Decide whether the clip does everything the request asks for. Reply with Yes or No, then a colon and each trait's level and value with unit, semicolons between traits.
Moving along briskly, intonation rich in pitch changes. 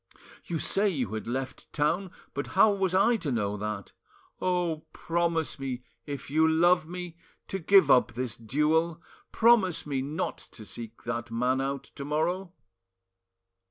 No: average, 155 wpm; wide, 5.7 semitones